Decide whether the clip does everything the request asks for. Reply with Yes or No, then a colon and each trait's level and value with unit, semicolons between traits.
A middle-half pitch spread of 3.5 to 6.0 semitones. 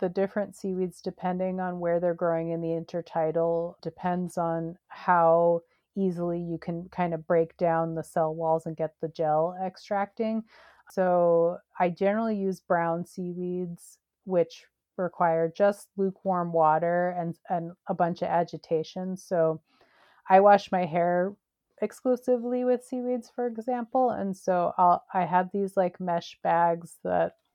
No: narrow, 2.5 semitones